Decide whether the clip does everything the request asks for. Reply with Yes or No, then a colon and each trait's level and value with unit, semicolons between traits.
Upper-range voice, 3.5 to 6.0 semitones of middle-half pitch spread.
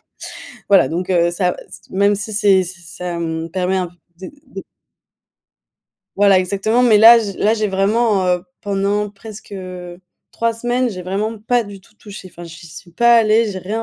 No: high, 195 Hz; average, 3.1 semitones